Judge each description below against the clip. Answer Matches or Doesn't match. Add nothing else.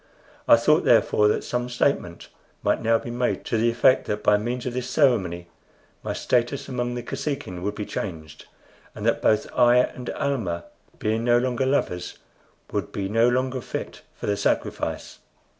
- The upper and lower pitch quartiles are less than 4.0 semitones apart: Matches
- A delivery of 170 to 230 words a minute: Matches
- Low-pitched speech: Matches